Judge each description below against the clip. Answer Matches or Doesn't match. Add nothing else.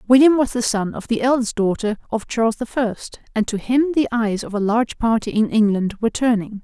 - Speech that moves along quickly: Matches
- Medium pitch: Doesn't match